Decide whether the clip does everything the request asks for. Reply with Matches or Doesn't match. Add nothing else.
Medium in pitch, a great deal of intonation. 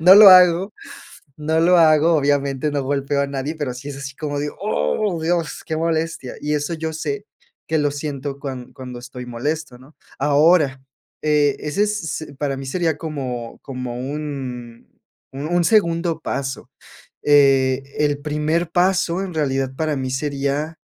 Doesn't match